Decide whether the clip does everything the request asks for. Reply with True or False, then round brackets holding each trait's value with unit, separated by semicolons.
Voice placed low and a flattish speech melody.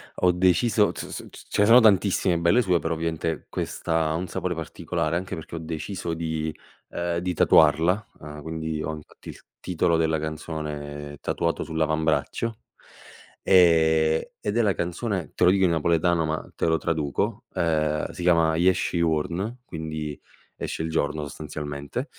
True (80 Hz; 2.3 semitones)